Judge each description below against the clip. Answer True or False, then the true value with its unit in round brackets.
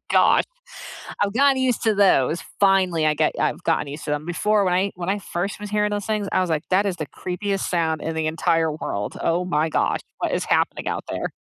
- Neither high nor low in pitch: True (180 Hz)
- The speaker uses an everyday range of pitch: True (4.1 semitones)